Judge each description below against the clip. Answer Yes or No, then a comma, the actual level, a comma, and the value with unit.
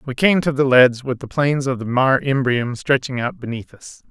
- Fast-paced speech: Yes, fast, 235 wpm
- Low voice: Yes, low, 130 Hz